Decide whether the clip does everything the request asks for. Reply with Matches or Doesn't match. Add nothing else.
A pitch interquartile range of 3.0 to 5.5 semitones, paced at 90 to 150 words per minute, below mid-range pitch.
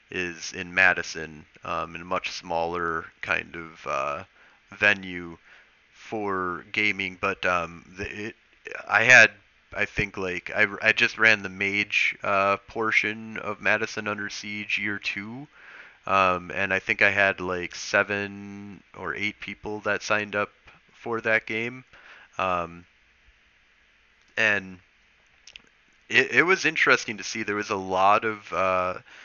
Doesn't match